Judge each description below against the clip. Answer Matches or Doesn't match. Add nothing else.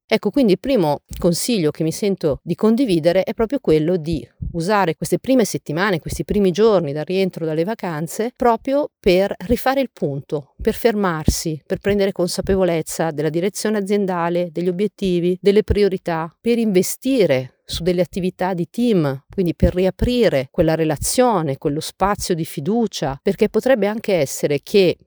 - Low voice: Doesn't match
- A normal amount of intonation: Matches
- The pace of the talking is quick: Doesn't match